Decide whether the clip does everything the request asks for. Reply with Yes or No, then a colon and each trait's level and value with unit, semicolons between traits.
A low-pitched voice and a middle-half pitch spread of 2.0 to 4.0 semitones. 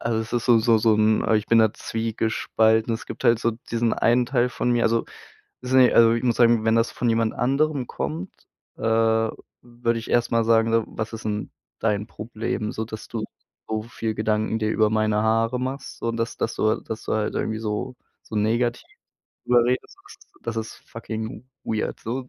No: low, 115 Hz; narrow, 1.4 semitones